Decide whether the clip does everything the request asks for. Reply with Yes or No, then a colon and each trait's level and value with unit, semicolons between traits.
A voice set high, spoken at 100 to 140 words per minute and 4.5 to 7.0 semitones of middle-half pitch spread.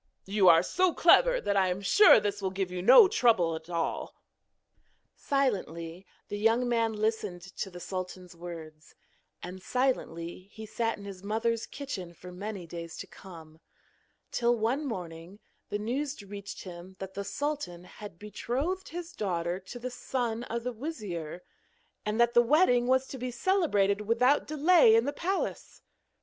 No: high, 210 Hz; average, 160 wpm; wide, 5.6 semitones